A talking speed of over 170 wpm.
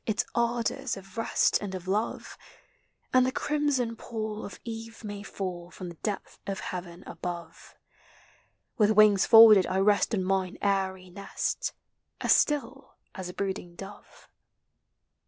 No: average, 140 wpm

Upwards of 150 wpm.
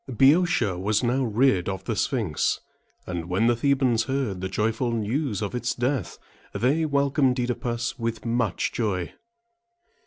No: average, 145 wpm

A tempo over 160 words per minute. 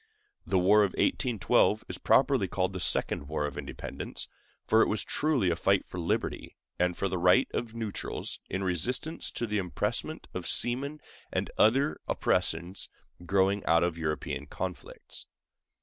No: average, 155 wpm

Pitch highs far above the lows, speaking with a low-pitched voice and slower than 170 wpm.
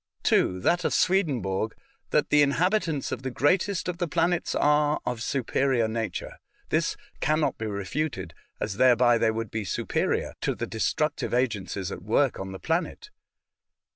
Yes: wide, 6.0 semitones; low, 130 Hz; average, 160 wpm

